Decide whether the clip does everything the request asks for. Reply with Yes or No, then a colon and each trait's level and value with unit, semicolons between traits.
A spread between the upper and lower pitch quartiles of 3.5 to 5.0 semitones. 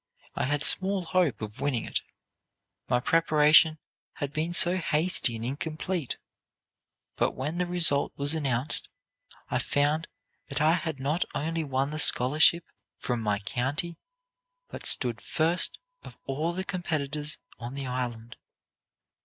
Yes: average, 4.0 semitones